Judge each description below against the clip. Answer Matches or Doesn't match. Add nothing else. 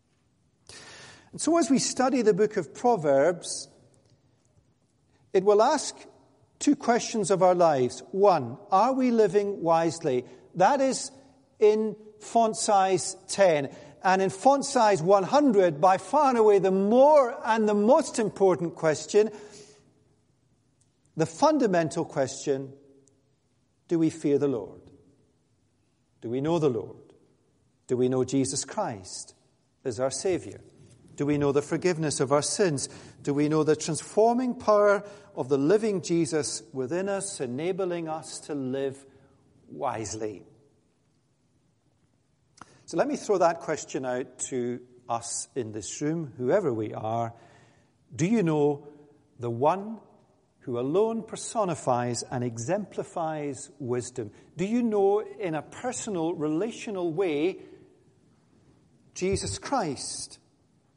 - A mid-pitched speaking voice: Matches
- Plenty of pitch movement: Matches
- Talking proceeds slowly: Matches